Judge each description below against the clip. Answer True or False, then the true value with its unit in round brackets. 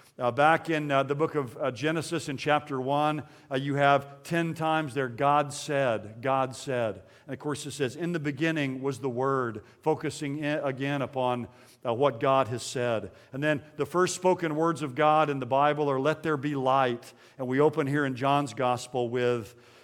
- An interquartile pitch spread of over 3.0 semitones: False (2.7 semitones)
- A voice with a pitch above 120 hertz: True (140 Hz)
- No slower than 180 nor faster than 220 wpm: True (200 wpm)